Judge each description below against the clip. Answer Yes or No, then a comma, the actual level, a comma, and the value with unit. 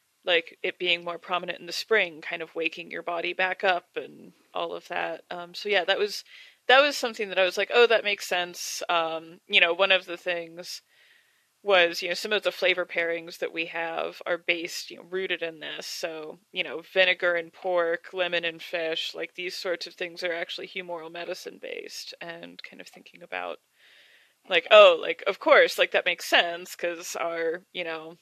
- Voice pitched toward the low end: No, medium, 180 Hz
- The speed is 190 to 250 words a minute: Yes, fast, 205 wpm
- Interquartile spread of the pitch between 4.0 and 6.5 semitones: No, average, 2.9 semitones